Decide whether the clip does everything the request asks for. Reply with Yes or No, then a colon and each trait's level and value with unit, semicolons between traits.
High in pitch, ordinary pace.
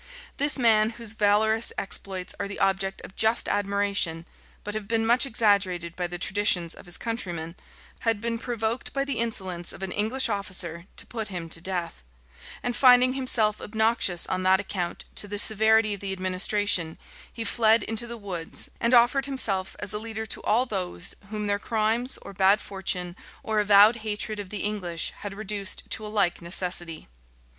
Yes: high, 205 Hz; average, 180 wpm